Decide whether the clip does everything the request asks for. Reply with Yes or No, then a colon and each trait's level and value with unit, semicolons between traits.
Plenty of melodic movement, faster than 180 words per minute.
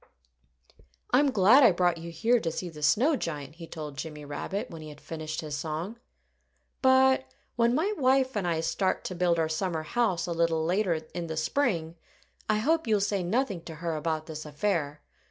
Yes: wide, 6.1 semitones; average, 190 wpm